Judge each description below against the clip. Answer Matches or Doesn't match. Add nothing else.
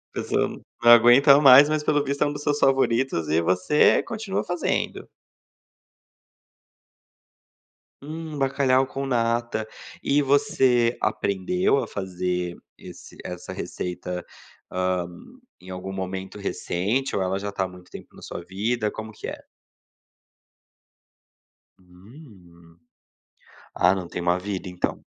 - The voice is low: Matches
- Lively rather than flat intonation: Matches